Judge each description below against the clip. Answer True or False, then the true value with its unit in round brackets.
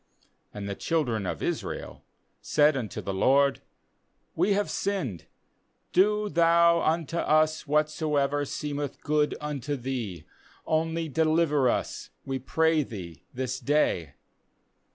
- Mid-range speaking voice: True (150 Hz)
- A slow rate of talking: True (120 wpm)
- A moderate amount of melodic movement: True (3.9 semitones)